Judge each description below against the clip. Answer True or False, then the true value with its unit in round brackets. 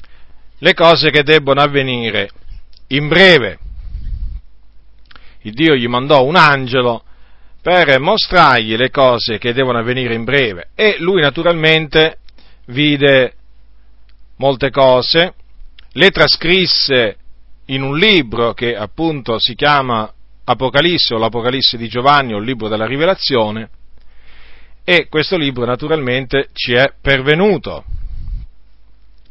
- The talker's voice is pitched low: True (125 Hz)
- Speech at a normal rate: False (110 wpm)